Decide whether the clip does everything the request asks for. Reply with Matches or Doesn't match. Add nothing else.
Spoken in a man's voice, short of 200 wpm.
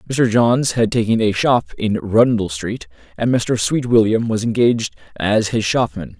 Matches